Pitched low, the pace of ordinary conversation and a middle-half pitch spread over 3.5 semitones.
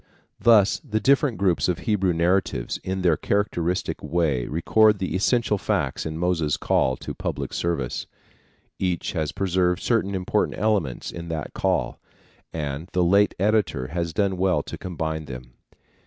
Yes: very low, 90 Hz; average, 150 wpm; average, 3.9 semitones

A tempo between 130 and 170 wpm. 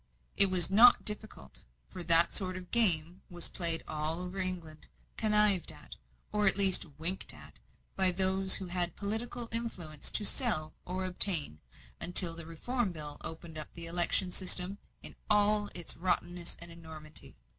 Yes: average, 155 wpm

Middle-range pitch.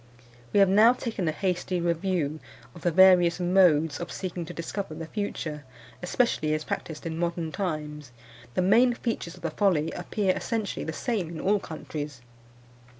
Yes: medium, 175 Hz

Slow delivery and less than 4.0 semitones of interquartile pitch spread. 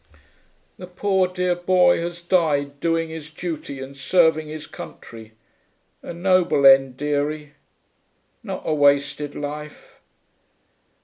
Yes: slow, 115 wpm; average, 3.5 semitones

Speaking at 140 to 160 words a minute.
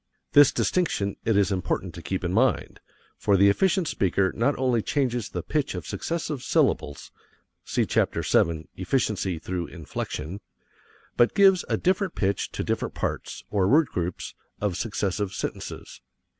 Yes: average, 150 wpm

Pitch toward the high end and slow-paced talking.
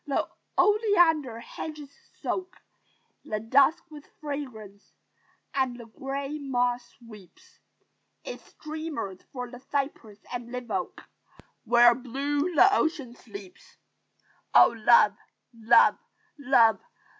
Yes: very high, 260 Hz; slow, 105 wpm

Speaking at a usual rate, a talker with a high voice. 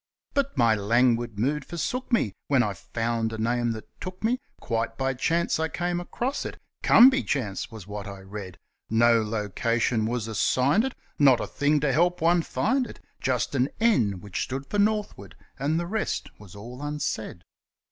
No: average, 180 wpm; low, 125 Hz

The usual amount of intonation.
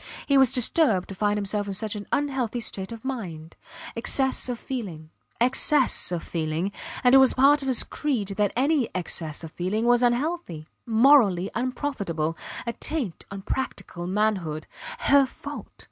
No: wide, 6.1 semitones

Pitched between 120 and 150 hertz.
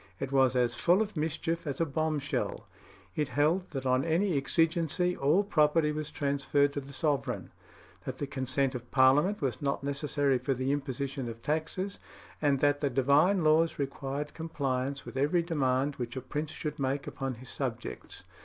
Yes: medium, 140 Hz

